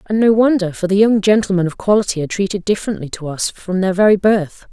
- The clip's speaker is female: Yes, female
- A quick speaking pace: Yes, fast, 230 wpm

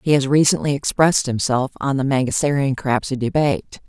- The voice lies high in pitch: No, low, 135 Hz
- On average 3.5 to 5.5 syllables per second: No, 5.7 syllables/s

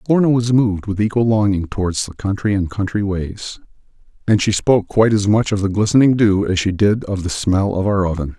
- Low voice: Yes, low, 100 Hz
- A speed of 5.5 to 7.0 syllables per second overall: Yes, 5.7 syllables/s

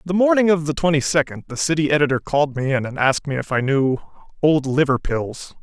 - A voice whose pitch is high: No, medium, 145 Hz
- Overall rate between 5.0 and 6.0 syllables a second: Yes, 5.9 syllables/s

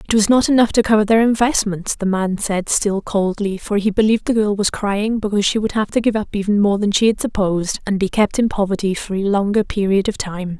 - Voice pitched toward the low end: No, high, 205 Hz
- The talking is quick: Yes, fast, 250 wpm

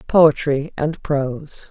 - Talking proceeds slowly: Yes, slow, 105 wpm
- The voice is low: No, medium, 150 Hz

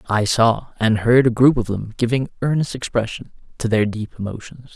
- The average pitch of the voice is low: Yes, low, 115 Hz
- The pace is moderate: Yes, average, 190 wpm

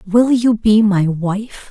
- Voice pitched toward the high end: Yes, high, 210 Hz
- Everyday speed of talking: Yes, average, 175 wpm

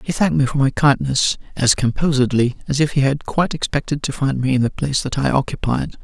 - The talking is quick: Yes, fast, 230 wpm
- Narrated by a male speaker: Yes, male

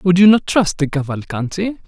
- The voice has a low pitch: No, medium, 175 Hz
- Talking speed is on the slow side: No, average, 190 wpm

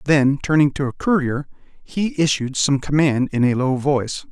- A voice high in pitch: No, medium, 140 Hz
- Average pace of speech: Yes, average, 180 wpm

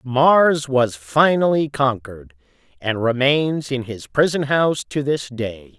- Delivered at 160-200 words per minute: No, slow, 135 wpm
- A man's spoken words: Yes, male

